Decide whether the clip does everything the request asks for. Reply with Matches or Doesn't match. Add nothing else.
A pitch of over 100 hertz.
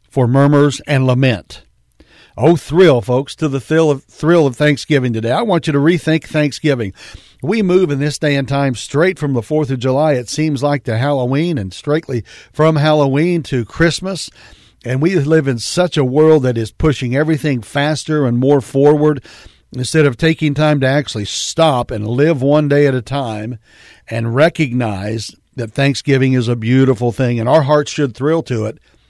Matches